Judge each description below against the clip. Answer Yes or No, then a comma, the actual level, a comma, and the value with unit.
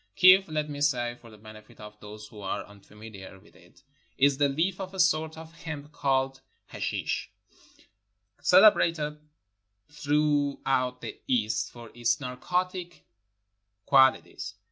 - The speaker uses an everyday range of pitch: No, wide, 5.9 semitones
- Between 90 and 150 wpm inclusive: Yes, slow, 135 wpm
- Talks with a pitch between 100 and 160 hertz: Yes, medium, 140 Hz